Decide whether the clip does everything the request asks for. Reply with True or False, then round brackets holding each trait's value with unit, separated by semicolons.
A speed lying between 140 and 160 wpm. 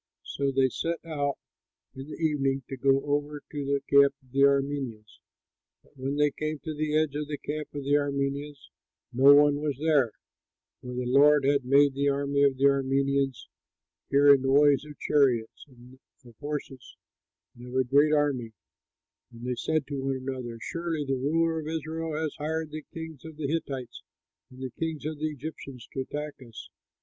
False (185 wpm)